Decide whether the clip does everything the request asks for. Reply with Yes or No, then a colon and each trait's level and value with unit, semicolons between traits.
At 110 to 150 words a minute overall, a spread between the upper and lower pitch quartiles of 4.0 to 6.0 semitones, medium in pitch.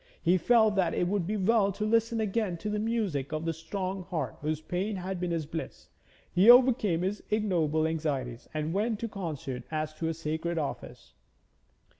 No: average, 190 wpm; average, 5.0 semitones; medium, 180 Hz